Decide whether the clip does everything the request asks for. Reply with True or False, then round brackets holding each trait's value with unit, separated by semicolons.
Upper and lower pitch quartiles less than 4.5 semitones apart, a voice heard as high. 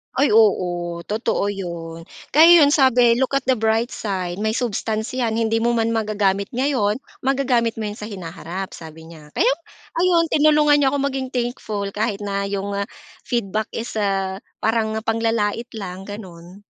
True (3.8 semitones; 220 Hz)